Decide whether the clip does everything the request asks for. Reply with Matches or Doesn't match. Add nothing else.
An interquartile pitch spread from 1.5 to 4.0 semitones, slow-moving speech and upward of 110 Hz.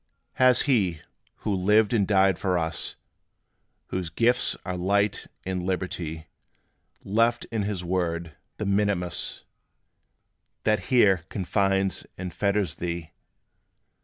Doesn't match